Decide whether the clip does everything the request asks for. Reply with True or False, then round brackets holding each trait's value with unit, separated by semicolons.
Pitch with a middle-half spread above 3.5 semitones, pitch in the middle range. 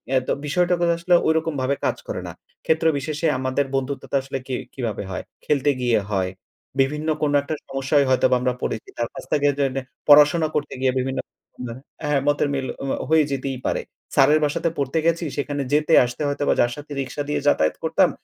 False (2.4 semitones; 145 Hz)